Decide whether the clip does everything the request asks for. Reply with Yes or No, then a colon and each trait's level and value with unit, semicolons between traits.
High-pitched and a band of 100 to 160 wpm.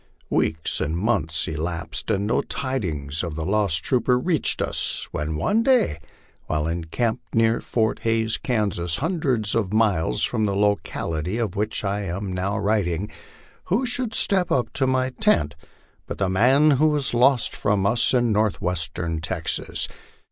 No: low, 105 Hz; average, 155 wpm